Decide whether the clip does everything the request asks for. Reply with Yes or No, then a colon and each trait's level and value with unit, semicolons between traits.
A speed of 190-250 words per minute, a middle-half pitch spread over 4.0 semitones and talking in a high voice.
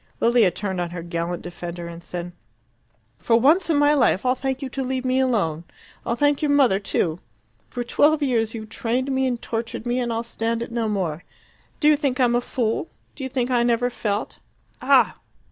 Yes: fast, 205 wpm; average, 4.6 semitones; high, 235 Hz